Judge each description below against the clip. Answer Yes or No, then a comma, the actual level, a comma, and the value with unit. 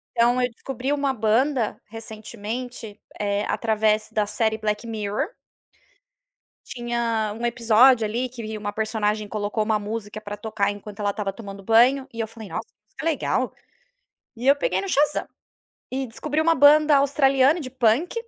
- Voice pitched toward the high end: Yes, high, 225 Hz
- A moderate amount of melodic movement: Yes, average, 3.4 semitones